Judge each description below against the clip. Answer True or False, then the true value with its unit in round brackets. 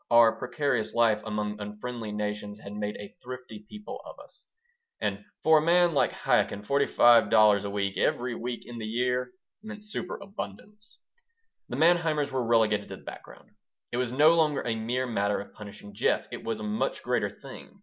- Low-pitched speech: True (120 Hz)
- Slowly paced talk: False (180 wpm)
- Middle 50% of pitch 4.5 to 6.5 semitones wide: True (5.1 semitones)